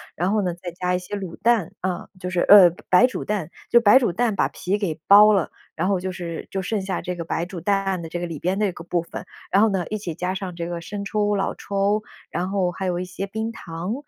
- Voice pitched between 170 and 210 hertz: Yes, medium, 185 Hz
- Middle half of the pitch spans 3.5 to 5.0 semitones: No, narrow, 2.5 semitones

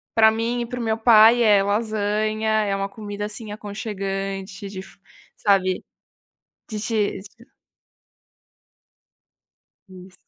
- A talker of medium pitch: No, high, 210 Hz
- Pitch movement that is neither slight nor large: No, narrow, 1.9 semitones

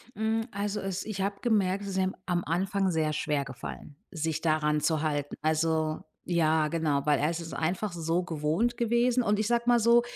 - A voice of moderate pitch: Yes, medium, 175 Hz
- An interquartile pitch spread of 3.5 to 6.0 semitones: Yes, average, 4.8 semitones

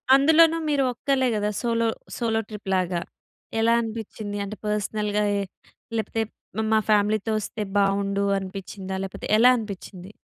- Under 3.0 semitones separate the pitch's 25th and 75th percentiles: Yes, narrow, 2.5 semitones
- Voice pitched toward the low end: No, high, 210 Hz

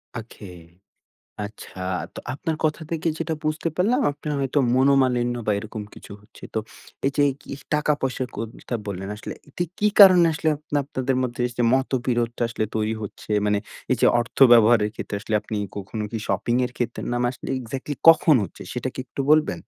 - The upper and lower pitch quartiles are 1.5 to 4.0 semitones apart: No, average, 4.9 semitones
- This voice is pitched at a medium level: No, low, 125 Hz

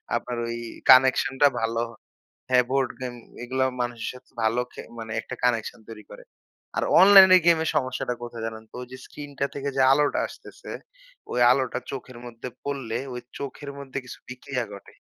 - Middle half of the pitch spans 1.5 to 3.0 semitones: Yes, average, 2.7 semitones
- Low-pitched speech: Yes, low, 130 Hz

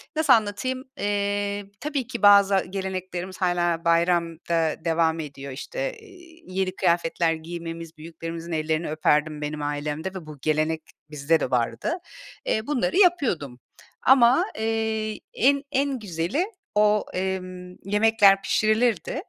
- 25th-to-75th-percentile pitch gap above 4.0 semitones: Yes, average, 5.3 semitones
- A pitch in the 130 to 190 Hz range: Yes, medium, 185 Hz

